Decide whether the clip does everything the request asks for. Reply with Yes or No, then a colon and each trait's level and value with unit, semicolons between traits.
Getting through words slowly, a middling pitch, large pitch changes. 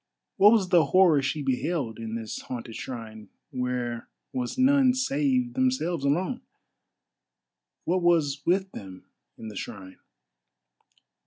Yes: slow, 120 wpm; medium, 150 Hz; wide, 8.8 semitones